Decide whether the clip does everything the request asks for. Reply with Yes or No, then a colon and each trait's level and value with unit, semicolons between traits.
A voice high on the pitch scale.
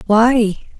Yes: high, 220 Hz